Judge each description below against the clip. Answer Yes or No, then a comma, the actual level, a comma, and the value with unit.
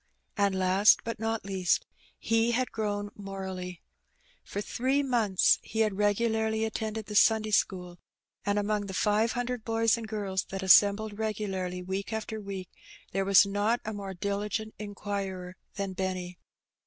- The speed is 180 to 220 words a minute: No, average, 150 wpm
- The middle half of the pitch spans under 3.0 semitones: Yes, narrow, 2.4 semitones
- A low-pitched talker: No, high, 205 Hz